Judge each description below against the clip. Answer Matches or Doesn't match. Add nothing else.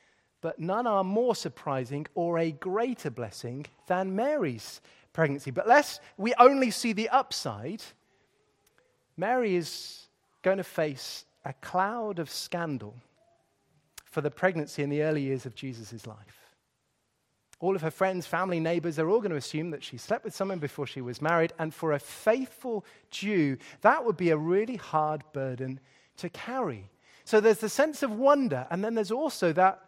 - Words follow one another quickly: Doesn't match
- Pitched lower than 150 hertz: Doesn't match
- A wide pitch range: Matches